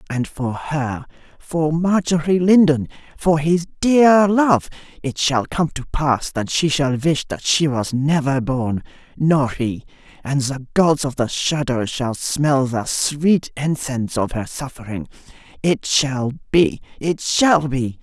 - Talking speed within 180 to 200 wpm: No, slow, 135 wpm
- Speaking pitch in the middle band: Yes, medium, 145 Hz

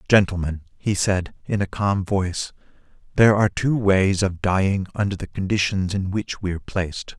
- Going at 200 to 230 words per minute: No, average, 165 wpm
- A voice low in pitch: Yes, very low, 95 Hz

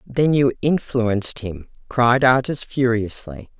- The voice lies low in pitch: Yes, low, 120 Hz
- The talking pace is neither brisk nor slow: No, slow, 115 wpm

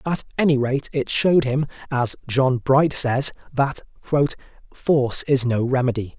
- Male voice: Yes, male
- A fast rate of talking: No, average, 145 wpm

